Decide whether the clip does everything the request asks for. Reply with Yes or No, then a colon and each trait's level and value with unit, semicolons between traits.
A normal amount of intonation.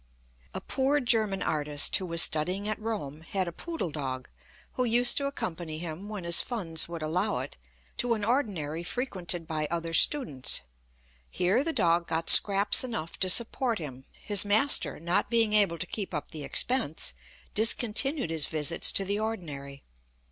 No: wide, 5.7 semitones